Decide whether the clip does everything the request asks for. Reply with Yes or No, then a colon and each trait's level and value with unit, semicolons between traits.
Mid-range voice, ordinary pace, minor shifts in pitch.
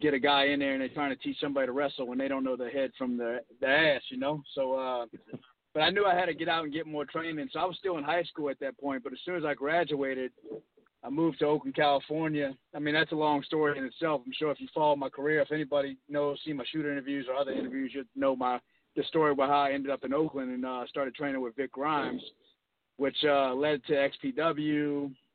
No: medium, 145 Hz; fast, 260 wpm; narrow, 2.3 semitones